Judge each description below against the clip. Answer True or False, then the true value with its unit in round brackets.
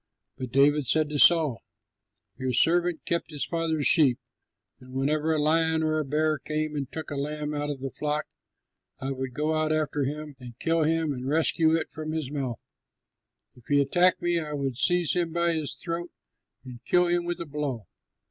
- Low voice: False (150 Hz)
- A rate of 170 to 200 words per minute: True (195 wpm)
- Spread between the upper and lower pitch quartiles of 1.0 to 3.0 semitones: True (2.7 semitones)